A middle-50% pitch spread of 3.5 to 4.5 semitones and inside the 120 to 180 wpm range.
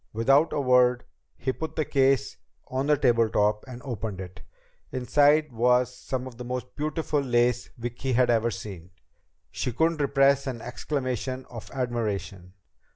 No: average, 2.8 semitones; average, 150 wpm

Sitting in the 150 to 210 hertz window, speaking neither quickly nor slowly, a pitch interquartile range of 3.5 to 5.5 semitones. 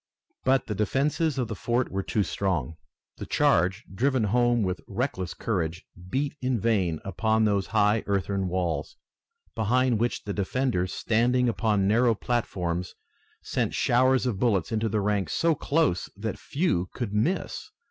No: low, 110 Hz; average, 145 wpm; average, 4.5 semitones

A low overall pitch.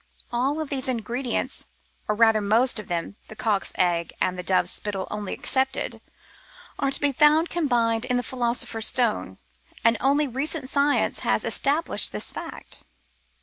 No: high, 245 Hz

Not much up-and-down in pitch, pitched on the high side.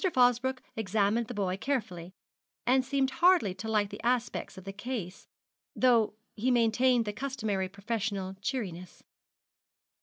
No: average, 4.3 semitones; high, 220 Hz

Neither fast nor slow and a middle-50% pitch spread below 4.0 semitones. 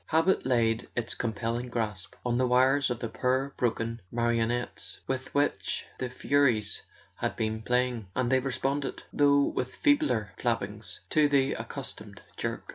Yes: average, 145 wpm; average, 2.9 semitones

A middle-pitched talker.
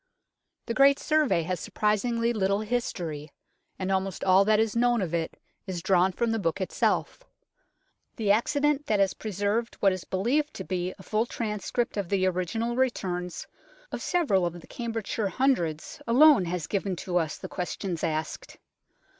No: high, 200 Hz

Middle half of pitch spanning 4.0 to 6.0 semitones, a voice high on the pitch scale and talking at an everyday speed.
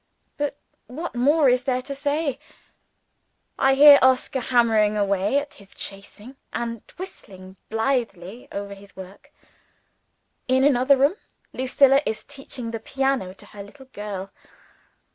No: average, 5.1 semitones; very high, 250 Hz; slow, 130 wpm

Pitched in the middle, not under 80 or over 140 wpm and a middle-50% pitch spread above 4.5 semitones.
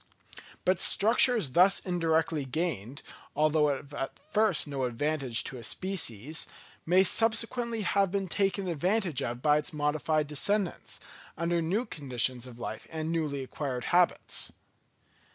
Yes: medium, 160 Hz; slow, 135 wpm; average, 5.2 semitones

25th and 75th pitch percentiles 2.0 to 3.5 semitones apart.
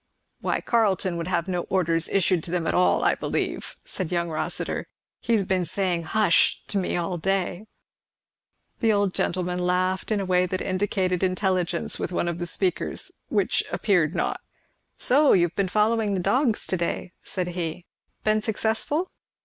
Yes: narrow, 2.5 semitones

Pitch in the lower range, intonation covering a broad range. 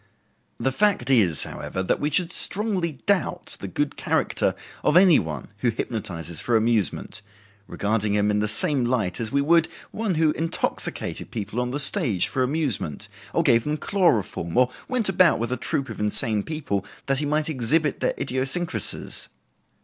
Yes: low, 130 Hz; wide, 7.0 semitones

